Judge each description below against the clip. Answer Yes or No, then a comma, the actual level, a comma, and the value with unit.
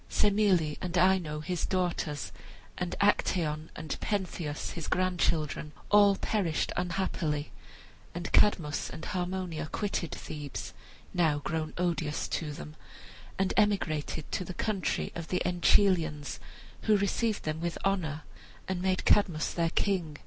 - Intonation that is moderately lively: Yes, average, 3.5 semitones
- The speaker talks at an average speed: No, slow, 125 wpm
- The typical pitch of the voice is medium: Yes, medium, 175 Hz